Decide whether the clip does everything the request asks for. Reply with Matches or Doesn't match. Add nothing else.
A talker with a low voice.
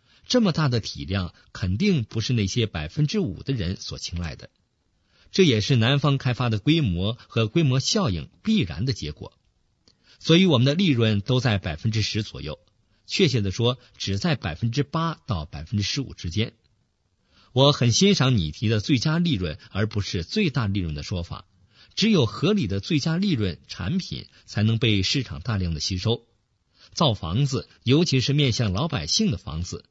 Matches